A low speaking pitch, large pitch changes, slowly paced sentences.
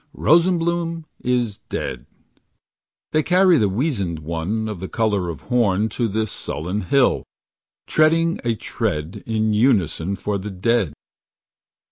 Yes: low, 110 Hz; wide, 6.5 semitones; slow, 125 wpm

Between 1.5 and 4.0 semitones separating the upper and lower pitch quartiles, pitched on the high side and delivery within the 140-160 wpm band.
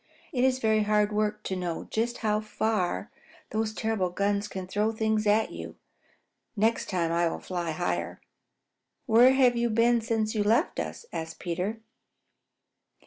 Yes: average, 3.1 semitones; high, 215 Hz; average, 155 wpm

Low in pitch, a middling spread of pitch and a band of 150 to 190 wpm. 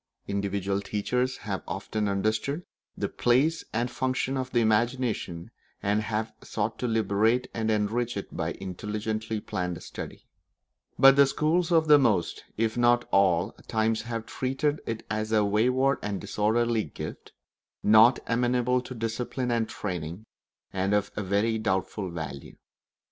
No: low, 110 Hz; average, 3.3 semitones; average, 140 wpm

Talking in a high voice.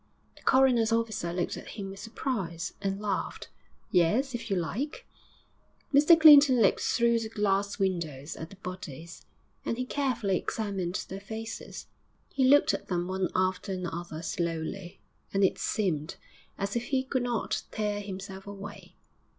Yes: high, 200 Hz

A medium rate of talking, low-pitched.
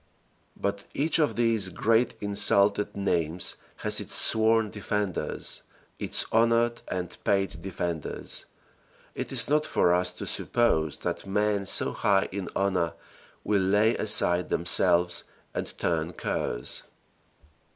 No: slow, 120 wpm; low, 100 Hz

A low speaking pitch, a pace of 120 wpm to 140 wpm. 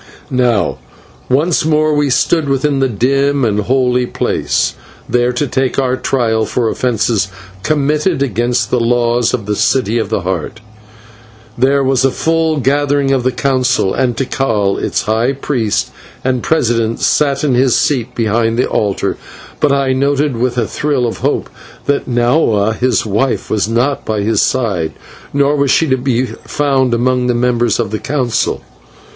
No: low, 125 Hz; average, 165 wpm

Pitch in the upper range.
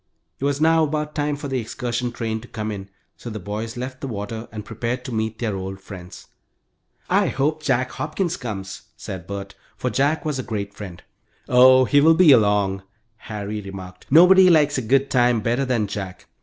No: low, 120 Hz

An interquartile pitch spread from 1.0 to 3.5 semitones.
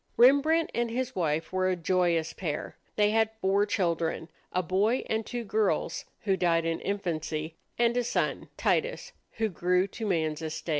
No: average, 5.2 semitones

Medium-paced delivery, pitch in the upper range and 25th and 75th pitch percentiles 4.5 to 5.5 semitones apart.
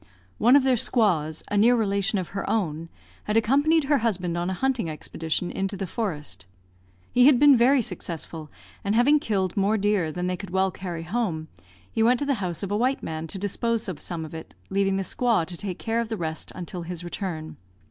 No: fast, 215 wpm; high, 195 Hz; average, 5.1 semitones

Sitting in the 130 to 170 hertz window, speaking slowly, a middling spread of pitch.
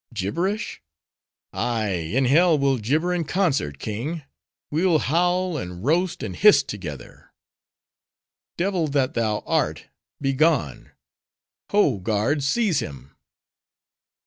No: medium, 140 Hz; slow, 105 wpm; wide, 8.3 semitones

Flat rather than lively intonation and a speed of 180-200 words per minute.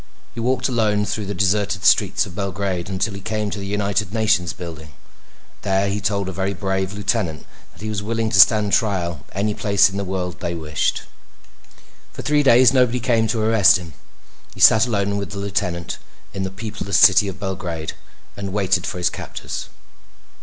Yes: narrow, 2.2 semitones; average, 185 wpm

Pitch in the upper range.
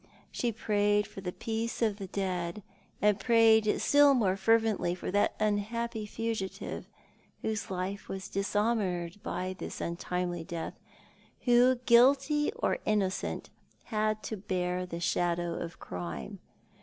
Yes: high, 205 Hz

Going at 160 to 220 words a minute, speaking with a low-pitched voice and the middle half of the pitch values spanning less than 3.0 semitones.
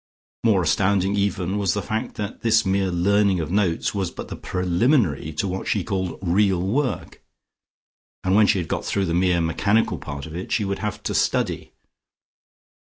Yes: average, 180 wpm; very low, 95 Hz; narrow, 2.6 semitones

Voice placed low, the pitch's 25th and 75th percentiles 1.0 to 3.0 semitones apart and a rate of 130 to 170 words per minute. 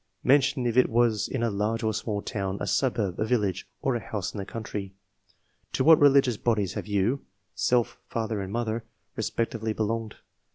No: low, 110 Hz; average, 2.7 semitones; average, 180 wpm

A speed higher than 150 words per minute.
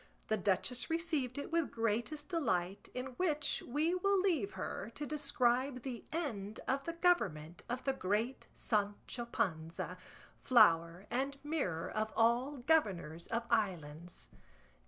No: slow, 135 wpm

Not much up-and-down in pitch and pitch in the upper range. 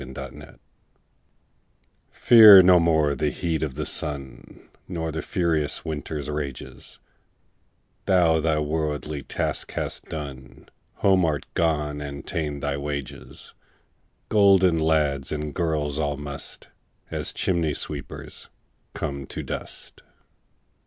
No: narrow, 2.3 semitones; very low, 75 Hz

